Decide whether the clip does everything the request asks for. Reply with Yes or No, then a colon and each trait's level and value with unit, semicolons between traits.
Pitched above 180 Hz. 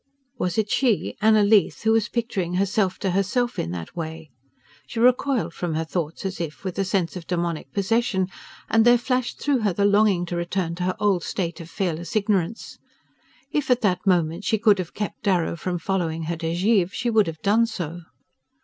Yes: high, 190 Hz